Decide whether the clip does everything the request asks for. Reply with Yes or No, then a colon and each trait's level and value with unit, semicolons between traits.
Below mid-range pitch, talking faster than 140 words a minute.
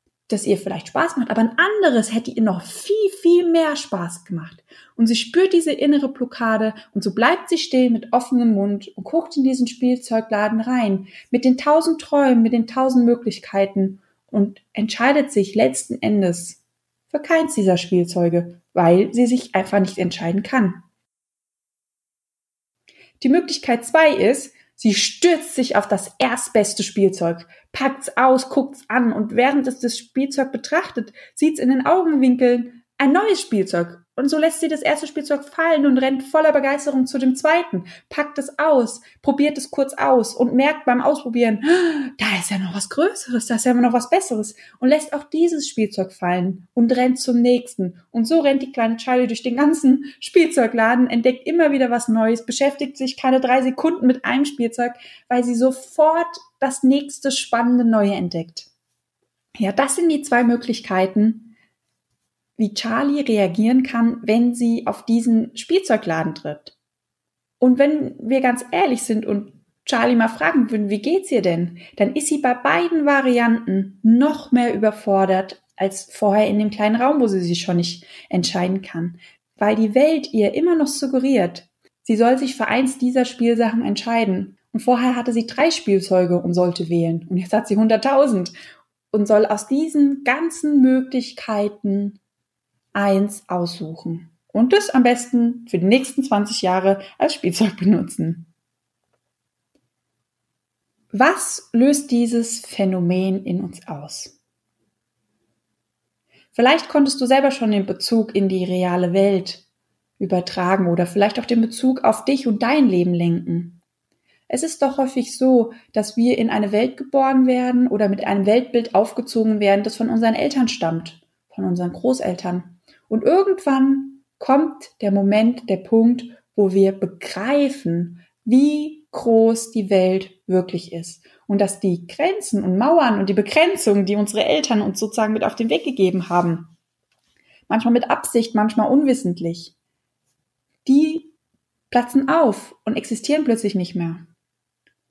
No: high, 235 Hz; average, 155 wpm